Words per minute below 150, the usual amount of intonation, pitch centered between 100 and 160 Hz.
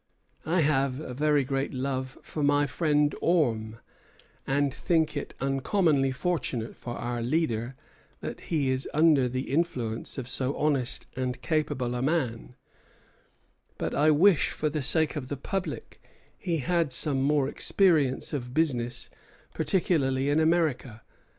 Yes: average, 140 wpm; average, 3.6 semitones; medium, 140 Hz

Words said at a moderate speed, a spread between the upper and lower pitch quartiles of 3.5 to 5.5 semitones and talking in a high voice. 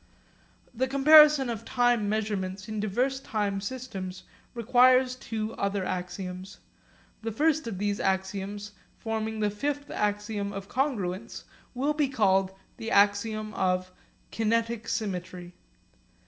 No: slow, 120 wpm; average, 3.9 semitones; high, 215 Hz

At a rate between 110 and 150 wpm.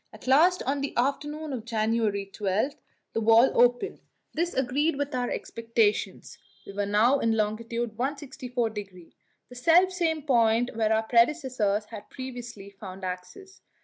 Yes: average, 140 wpm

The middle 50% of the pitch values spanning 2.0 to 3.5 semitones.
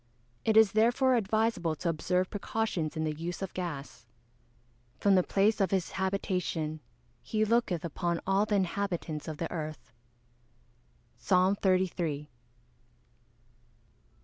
No: average, 4.0 semitones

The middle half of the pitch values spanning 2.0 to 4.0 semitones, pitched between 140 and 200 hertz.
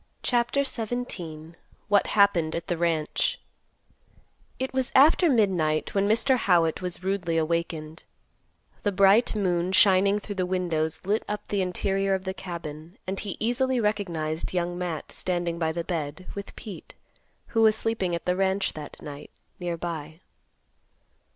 Yes: average, 3.6 semitones; medium, 185 Hz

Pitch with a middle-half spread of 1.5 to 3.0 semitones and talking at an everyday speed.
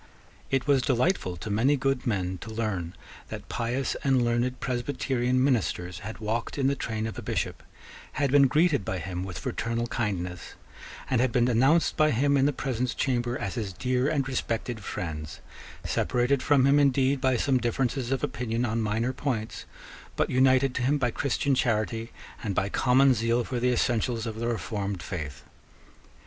No: average, 3.4 semitones; average, 175 wpm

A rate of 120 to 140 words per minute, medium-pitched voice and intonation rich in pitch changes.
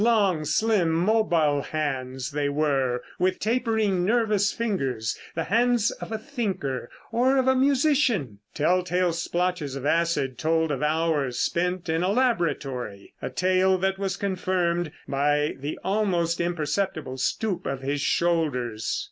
Yes: slow, 135 wpm; medium, 170 Hz; wide, 5.7 semitones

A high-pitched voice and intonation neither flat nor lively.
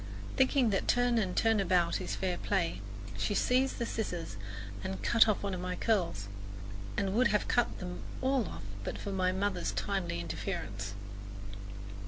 Yes: high, 195 Hz; average, 4.4 semitones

